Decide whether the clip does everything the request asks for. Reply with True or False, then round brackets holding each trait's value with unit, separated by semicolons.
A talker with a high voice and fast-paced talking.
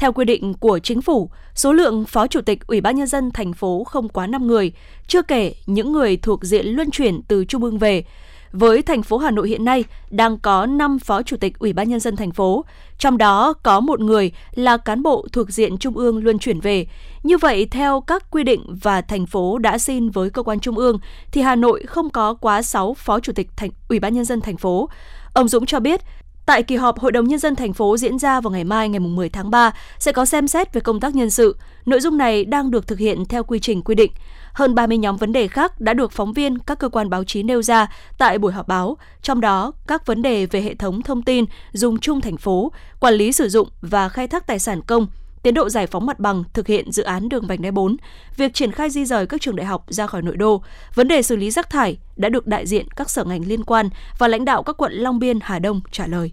True (230 Hz; 255 wpm)